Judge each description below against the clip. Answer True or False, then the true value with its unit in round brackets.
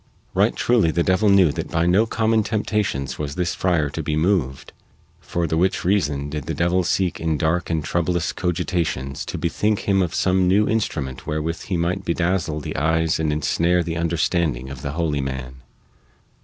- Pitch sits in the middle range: False (85 Hz)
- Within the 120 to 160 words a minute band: False (185 wpm)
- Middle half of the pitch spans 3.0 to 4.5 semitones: True (3.3 semitones)